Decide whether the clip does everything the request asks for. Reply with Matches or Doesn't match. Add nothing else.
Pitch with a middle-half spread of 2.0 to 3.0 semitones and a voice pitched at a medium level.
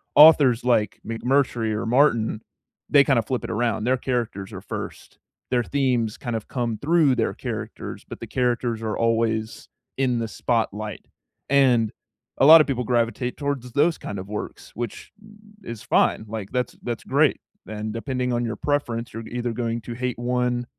Doesn't match